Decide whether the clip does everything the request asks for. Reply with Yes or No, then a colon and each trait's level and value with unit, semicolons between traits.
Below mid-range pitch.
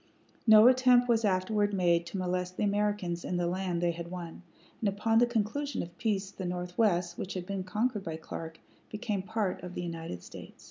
No: high, 190 Hz